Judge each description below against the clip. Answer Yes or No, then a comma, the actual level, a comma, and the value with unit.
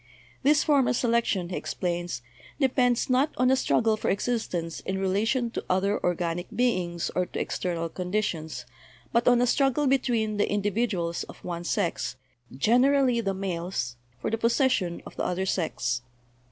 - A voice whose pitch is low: No, high, 200 Hz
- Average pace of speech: Yes, average, 165 wpm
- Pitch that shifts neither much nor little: No, wide, 5.8 semitones